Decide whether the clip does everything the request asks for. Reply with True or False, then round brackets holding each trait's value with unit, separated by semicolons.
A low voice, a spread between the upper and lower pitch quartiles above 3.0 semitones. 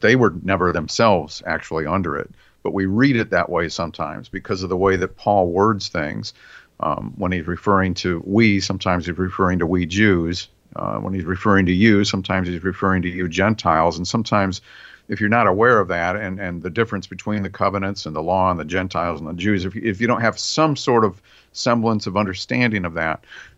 False (95 Hz; 2.6 semitones)